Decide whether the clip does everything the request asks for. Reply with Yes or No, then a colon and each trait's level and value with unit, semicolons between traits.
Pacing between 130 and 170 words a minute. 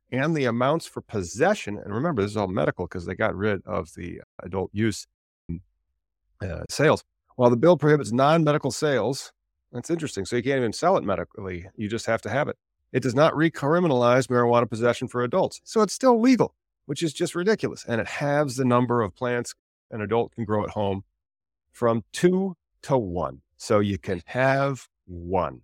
No: average, 190 wpm